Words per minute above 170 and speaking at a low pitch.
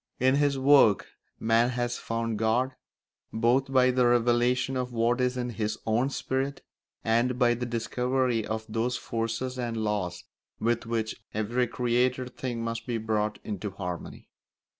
No: average, 150 wpm; low, 120 Hz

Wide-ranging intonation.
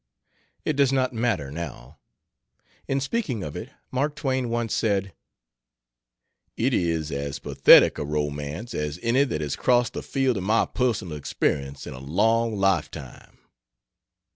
Yes: wide, 9.0 semitones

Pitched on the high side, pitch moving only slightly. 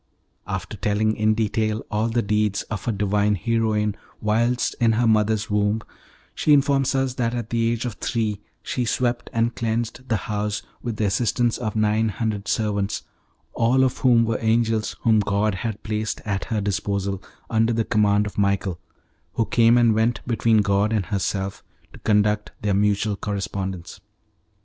No: low, 110 Hz; narrow, 2.0 semitones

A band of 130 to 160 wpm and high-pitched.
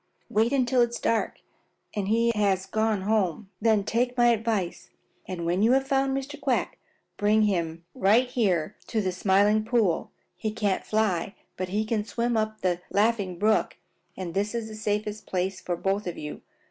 No: average, 185 wpm; high, 210 Hz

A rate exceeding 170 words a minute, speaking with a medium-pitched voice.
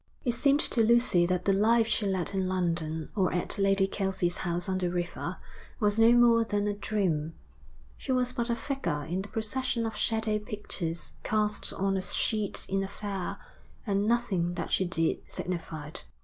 No: average, 180 wpm; high, 195 Hz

